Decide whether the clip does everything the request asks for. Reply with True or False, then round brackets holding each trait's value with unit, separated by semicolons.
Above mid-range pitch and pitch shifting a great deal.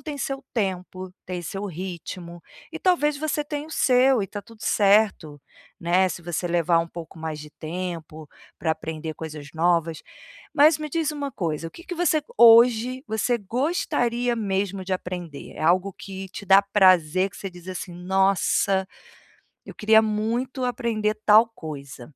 True (195 Hz; 5.8 semitones)